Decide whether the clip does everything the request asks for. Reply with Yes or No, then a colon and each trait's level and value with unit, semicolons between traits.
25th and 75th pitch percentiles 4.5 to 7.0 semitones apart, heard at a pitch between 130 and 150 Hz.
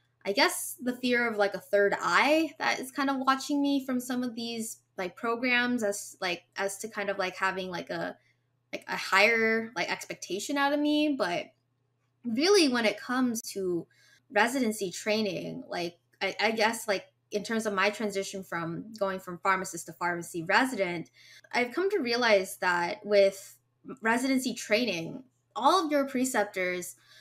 No: average, 5.0 semitones; high, 210 Hz